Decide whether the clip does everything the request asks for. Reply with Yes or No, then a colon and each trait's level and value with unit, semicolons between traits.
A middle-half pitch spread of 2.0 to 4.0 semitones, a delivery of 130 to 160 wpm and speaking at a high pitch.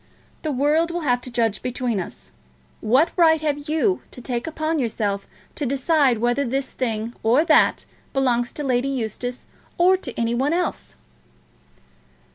No: average, 4.5 semitones; average, 155 wpm; very high, 260 Hz